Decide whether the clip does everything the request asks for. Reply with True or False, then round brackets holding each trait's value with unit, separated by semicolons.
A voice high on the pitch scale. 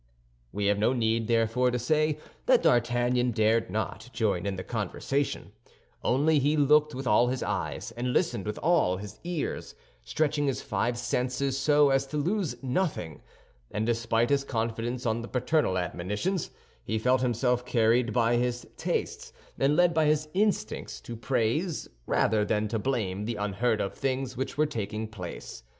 False (120 Hz)